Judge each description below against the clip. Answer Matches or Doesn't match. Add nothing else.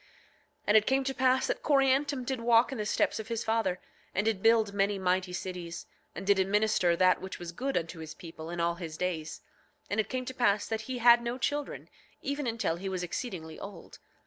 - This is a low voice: Doesn't match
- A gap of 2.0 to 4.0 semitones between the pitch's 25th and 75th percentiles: Doesn't match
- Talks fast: Matches